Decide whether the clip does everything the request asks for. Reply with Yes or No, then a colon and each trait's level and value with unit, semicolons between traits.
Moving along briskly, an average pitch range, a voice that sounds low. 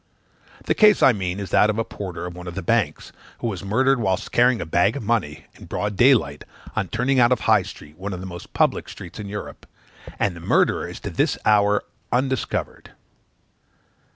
Yes: fast, 210 wpm; average, 4.8 semitones; low, 105 Hz